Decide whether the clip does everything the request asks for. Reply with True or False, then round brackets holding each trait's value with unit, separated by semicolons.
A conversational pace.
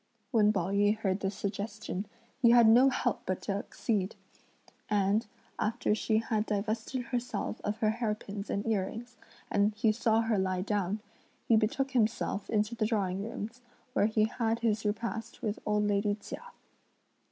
True (165 wpm)